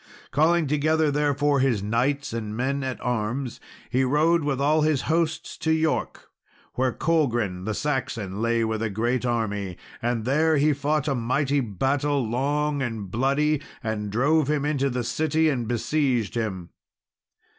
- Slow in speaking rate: No, average, 155 wpm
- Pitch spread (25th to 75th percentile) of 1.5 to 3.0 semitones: No, average, 4.4 semitones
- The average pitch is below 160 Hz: Yes, low, 135 Hz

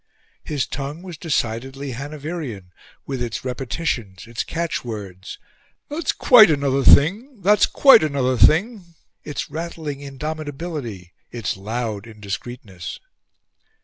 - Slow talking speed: Yes, slow, 105 wpm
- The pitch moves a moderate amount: No, wide, 5.8 semitones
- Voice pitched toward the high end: No, medium, 140 Hz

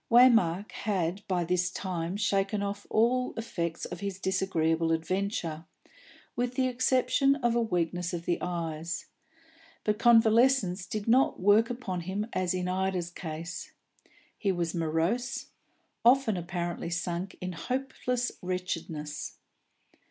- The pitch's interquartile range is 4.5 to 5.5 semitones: Yes, average, 4.9 semitones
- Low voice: No, medium, 185 Hz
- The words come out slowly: Yes, slow, 125 wpm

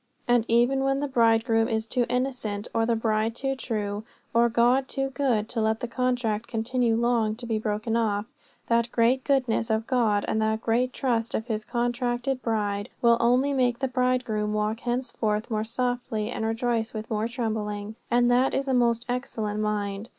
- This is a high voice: Yes, high, 235 Hz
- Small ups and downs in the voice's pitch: Yes, narrow, 2.2 semitones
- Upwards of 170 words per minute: Yes, average, 180 wpm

